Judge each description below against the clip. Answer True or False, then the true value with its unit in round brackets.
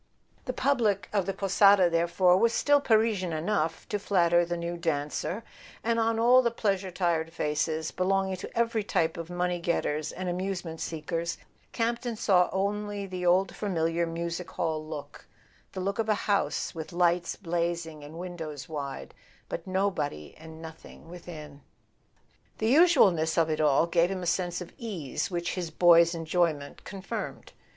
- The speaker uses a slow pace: False (160 wpm)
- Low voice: False (175 Hz)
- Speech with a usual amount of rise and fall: True (3.4 semitones)